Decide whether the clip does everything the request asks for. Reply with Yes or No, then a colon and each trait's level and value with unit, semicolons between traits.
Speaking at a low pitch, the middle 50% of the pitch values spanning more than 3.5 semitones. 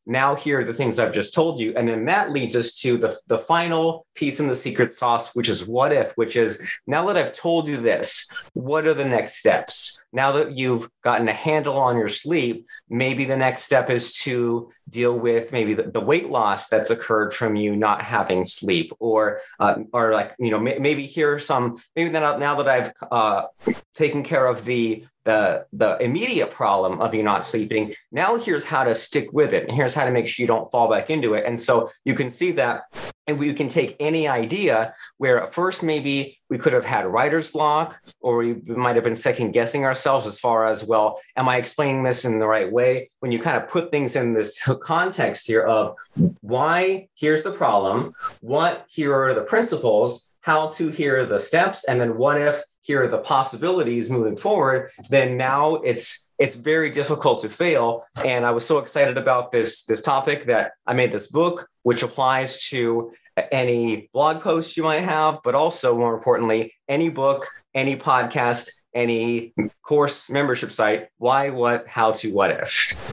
Yes: low, 130 Hz; average, 4.3 semitones